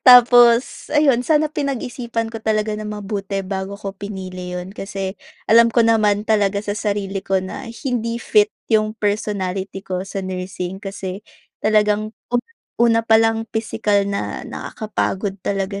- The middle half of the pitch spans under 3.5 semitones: Yes, average, 2.7 semitones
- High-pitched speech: Yes, high, 210 Hz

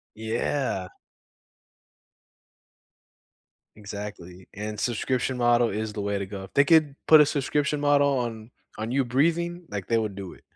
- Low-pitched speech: Yes, low, 120 Hz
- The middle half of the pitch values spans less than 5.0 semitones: No, wide, 5.5 semitones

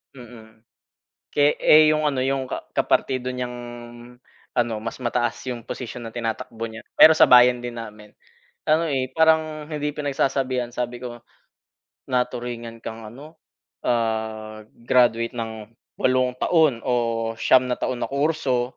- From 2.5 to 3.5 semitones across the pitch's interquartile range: Yes, average, 2.9 semitones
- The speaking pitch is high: No, low, 125 Hz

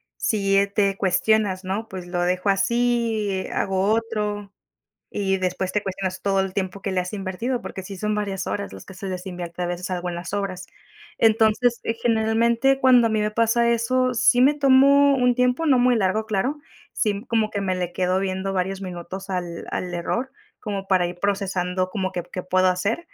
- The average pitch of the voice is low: No, high, 200 Hz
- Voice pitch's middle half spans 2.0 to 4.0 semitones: Yes, average, 3.5 semitones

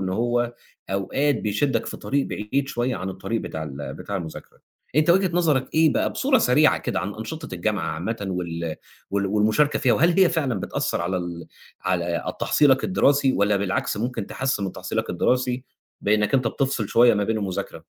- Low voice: Yes, low, 110 Hz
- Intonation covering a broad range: Yes, wide, 6.0 semitones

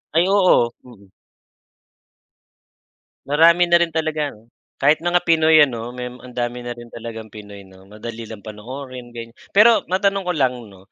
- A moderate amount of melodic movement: No, wide, 6.1 semitones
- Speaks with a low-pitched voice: Yes, low, 125 Hz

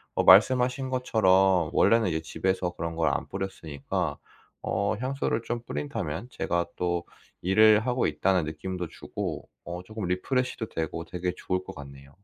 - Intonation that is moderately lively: Yes, average, 4.9 semitones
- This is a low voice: Yes, very low, 95 Hz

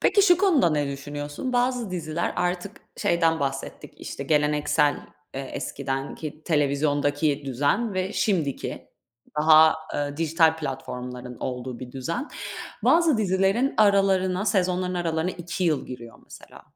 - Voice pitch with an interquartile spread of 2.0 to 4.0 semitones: No, average, 4.8 semitones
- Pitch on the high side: No, medium, 160 Hz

